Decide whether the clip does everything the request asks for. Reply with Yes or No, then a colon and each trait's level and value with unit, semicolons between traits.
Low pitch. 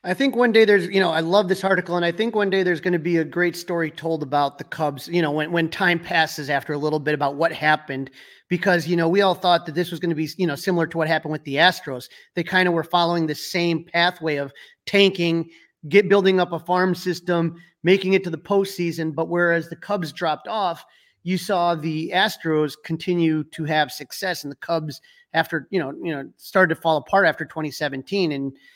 No: medium, 170 Hz